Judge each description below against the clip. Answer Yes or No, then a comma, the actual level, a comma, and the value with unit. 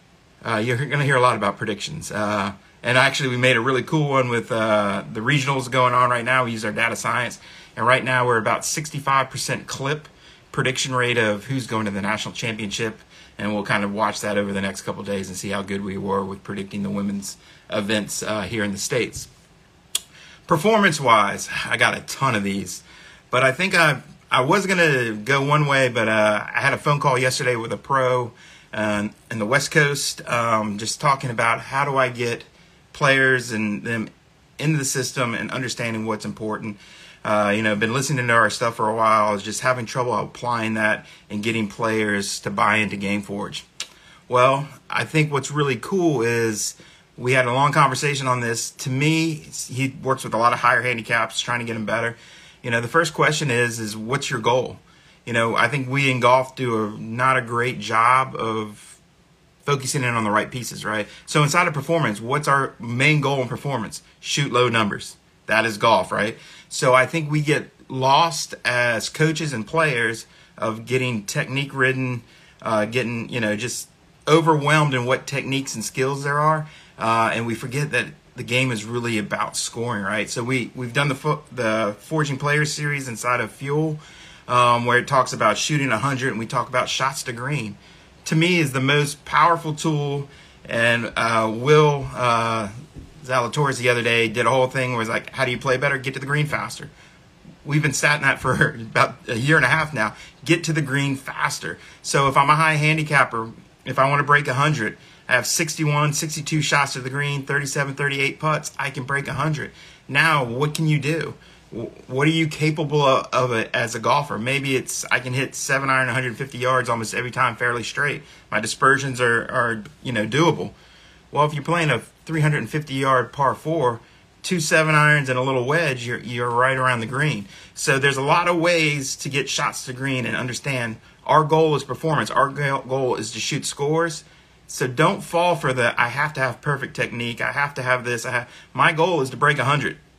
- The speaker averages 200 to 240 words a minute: Yes, fast, 205 wpm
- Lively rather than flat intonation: No, average, 4.2 semitones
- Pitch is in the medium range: No, low, 130 Hz